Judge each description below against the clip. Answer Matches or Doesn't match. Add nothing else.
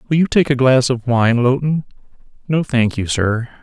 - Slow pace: Doesn't match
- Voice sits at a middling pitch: Doesn't match